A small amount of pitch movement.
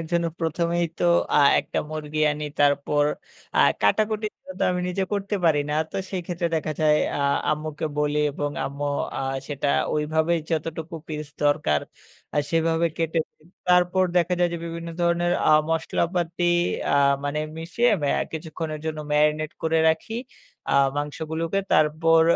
Yes: narrow, 2.2 semitones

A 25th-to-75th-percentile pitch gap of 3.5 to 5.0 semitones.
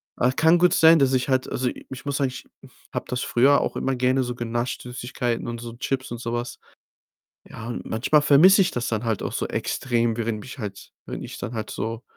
No: narrow, 2.5 semitones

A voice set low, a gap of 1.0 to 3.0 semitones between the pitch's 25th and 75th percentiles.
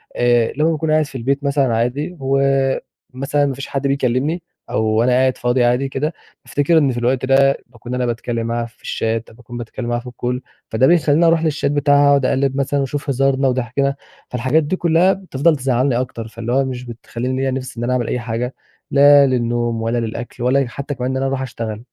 Yes: low, 130 Hz; average, 2.7 semitones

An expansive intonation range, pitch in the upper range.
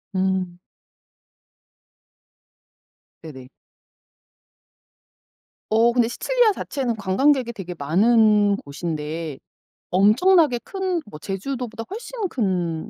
Yes: wide, 7.0 semitones; high, 210 Hz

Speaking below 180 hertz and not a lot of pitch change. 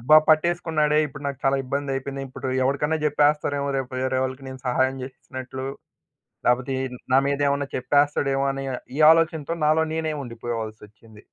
Yes: low, 135 Hz; narrow, 2.3 semitones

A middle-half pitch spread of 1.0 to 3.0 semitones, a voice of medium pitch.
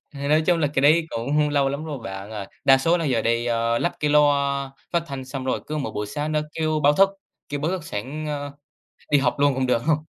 Yes: narrow, 2.4 semitones; medium, 145 Hz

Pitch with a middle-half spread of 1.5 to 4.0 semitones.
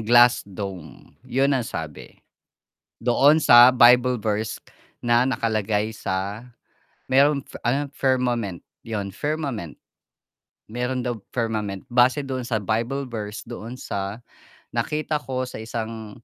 Yes: average, 3.3 semitones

